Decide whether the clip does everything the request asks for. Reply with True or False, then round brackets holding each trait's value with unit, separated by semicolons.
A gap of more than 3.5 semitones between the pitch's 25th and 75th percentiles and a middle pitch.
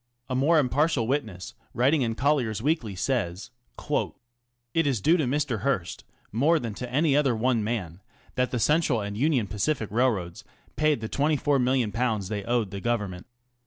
False (5.1 semitones; 125 Hz)